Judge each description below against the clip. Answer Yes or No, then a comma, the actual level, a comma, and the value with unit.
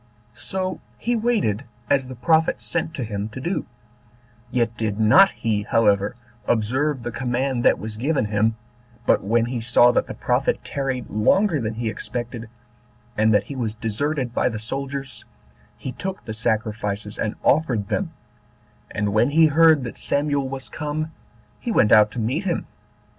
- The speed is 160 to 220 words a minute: Yes, average, 170 wpm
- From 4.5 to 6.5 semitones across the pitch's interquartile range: Yes, average, 4.8 semitones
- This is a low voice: Yes, low, 120 Hz